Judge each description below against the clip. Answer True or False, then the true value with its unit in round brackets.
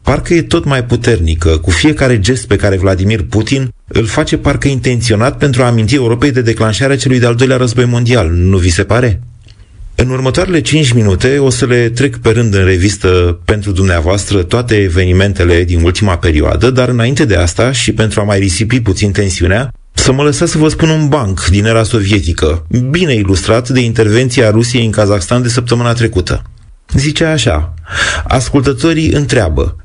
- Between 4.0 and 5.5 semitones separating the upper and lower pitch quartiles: True (5.0 semitones)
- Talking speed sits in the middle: False (175 wpm)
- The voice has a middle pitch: False (115 Hz)